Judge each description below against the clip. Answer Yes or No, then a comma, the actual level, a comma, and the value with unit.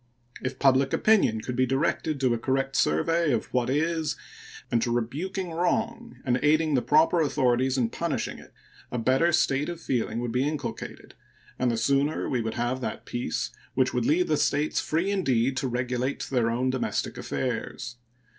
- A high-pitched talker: No, low, 130 Hz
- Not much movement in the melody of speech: No, average, 4.1 semitones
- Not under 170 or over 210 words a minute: Yes, average, 175 wpm